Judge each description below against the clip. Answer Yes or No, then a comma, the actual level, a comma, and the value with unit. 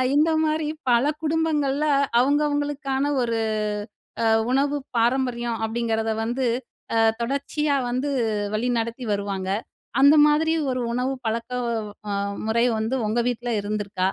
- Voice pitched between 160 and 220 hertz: No, very high, 250 Hz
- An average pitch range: Yes, average, 4.0 semitones